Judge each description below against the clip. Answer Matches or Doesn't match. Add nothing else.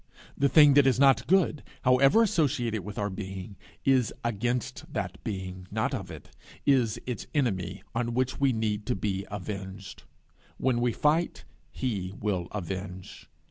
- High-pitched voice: Doesn't match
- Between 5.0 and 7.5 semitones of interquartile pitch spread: Matches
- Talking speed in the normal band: Matches